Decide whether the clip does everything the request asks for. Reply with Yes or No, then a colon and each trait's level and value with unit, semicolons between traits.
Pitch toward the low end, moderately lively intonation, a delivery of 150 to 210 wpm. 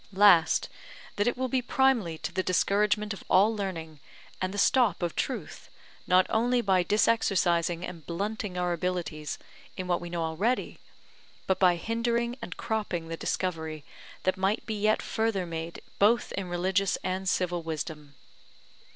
No: medium, 185 Hz; average, 3.9 semitones; average, 155 wpm